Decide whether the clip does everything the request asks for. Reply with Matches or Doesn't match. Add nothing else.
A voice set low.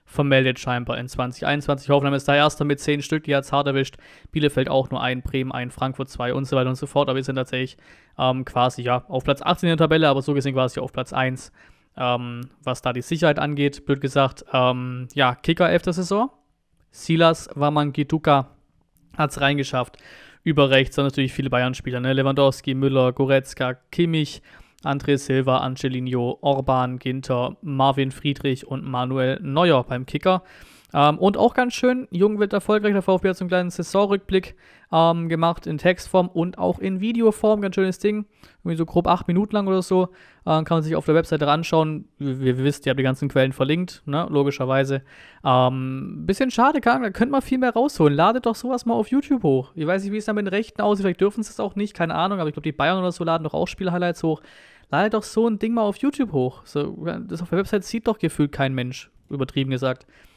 Doesn't match